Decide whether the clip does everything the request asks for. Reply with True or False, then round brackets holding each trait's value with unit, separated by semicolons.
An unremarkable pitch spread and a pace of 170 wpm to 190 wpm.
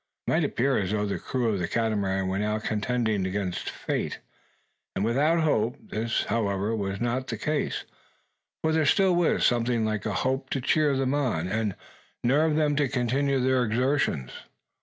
True (4.7 semitones; 175 wpm)